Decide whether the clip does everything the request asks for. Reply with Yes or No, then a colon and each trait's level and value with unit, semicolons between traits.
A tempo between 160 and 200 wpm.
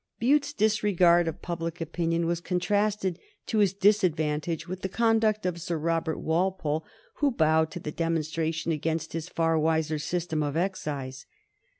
No: average, 150 wpm